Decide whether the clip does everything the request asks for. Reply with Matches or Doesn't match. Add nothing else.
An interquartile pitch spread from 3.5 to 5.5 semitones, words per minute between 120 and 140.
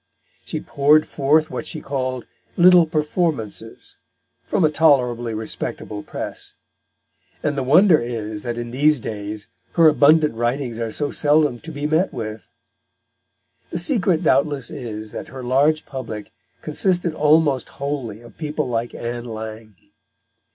Matches